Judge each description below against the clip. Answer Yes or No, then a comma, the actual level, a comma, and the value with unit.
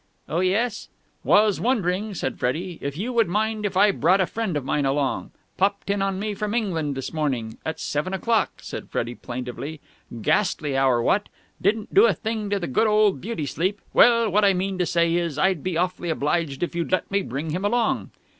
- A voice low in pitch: No, medium, 185 Hz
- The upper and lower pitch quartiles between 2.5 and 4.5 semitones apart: No, wide, 5.4 semitones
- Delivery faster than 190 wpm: Yes, fast, 205 wpm